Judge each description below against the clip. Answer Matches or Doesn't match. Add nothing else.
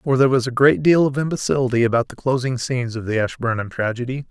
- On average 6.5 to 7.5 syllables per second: Matches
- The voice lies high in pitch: Doesn't match